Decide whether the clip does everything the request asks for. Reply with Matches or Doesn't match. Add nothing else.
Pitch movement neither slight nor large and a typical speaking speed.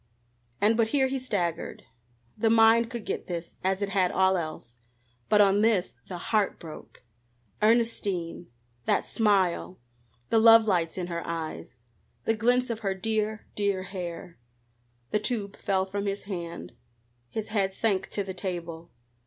Matches